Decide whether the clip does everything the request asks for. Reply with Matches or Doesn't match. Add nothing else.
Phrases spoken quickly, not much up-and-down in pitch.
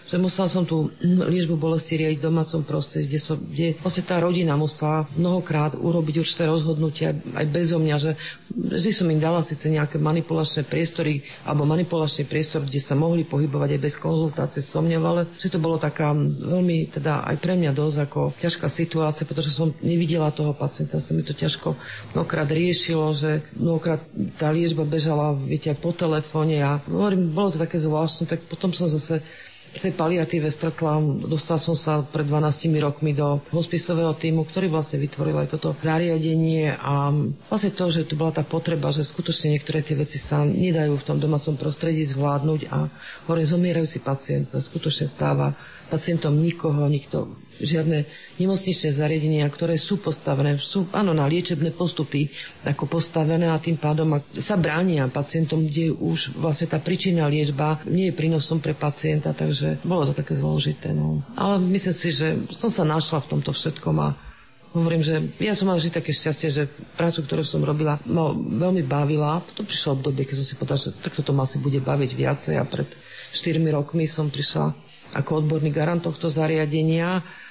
Matches